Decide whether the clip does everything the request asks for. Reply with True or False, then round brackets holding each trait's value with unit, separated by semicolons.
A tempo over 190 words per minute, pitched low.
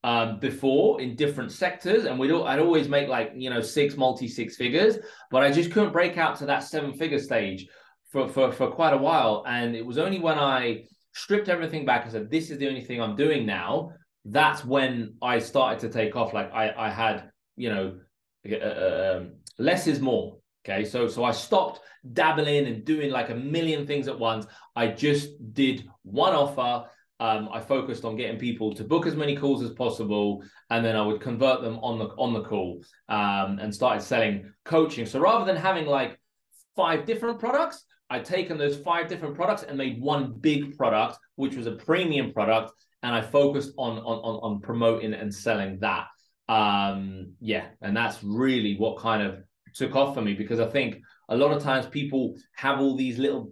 True (200 wpm; 130 Hz)